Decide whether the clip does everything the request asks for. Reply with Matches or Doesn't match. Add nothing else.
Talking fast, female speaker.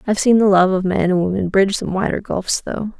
Matches